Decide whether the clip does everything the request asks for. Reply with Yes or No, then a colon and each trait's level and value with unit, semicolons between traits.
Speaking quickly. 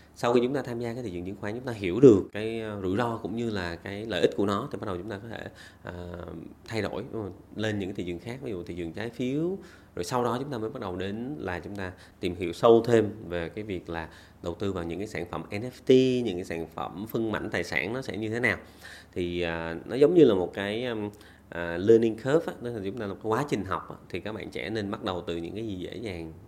Yes: fast, 285 wpm